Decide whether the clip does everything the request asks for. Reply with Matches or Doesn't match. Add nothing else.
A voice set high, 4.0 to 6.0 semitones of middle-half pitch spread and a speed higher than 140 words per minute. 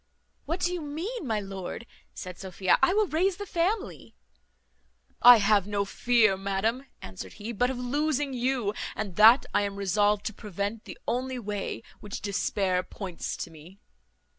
Matches